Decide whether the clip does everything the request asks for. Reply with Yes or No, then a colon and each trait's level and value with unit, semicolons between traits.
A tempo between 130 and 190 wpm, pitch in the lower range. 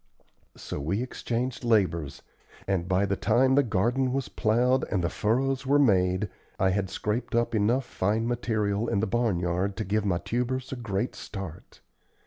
Yes: average, 165 wpm; low, 110 Hz